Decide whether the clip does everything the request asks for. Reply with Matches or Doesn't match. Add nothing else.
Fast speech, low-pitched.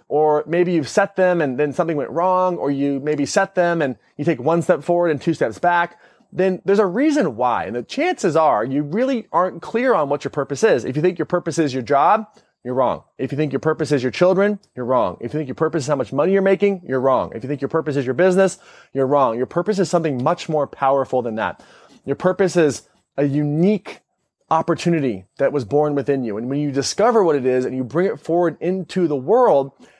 Doesn't match